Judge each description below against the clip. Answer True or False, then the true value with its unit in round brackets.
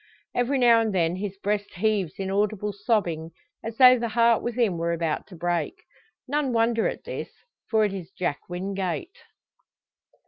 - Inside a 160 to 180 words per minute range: True (165 wpm)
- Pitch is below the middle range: False (205 Hz)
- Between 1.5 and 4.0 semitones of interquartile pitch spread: False (4.5 semitones)